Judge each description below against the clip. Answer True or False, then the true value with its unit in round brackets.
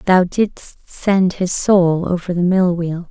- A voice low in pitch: False (180 Hz)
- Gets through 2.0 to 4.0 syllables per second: True (3.4 syllables/s)